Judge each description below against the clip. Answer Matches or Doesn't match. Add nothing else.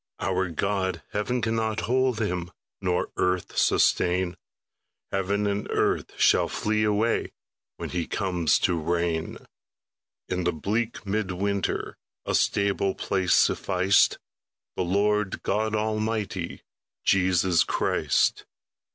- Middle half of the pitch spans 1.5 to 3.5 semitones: Matches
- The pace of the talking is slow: Matches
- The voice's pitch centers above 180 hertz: Doesn't match